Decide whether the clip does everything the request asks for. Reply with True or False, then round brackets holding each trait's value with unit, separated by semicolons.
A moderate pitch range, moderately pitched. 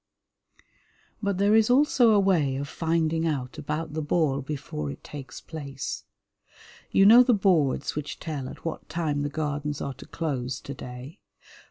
True (3.8 semitones; 150 Hz)